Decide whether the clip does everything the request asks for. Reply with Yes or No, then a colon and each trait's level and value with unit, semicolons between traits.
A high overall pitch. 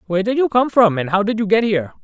Yes: high, 205 Hz